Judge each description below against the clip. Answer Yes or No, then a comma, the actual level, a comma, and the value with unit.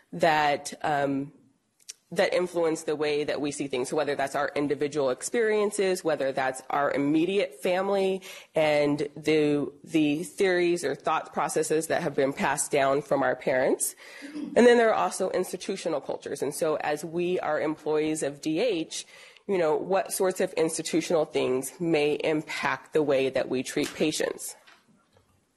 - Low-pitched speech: No, medium, 160 Hz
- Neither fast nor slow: Yes, average, 155 wpm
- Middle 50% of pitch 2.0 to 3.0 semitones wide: No, average, 4.6 semitones